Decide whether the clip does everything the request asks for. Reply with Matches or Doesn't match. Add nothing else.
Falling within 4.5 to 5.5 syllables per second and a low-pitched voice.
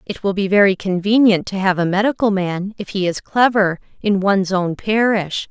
Doesn't match